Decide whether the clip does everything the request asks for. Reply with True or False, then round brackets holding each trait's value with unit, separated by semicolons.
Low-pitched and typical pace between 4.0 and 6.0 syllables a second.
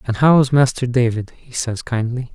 True (125 Hz; 5.1 syllables/s)